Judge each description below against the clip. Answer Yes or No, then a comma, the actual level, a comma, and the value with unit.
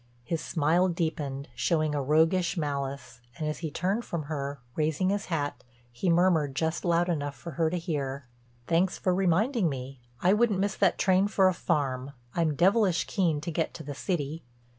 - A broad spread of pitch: No, average, 4.1 semitones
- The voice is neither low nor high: Yes, medium, 165 Hz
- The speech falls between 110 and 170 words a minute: No, average, 180 wpm